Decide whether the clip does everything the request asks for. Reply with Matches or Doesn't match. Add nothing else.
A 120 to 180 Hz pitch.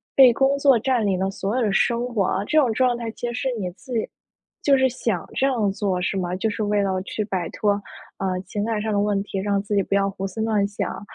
Doesn't match